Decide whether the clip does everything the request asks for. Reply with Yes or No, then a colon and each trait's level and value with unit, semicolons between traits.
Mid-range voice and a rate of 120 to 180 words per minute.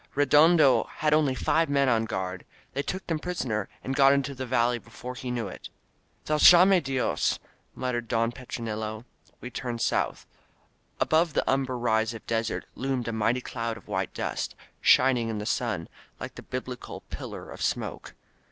No: low, 125 Hz; average, 170 wpm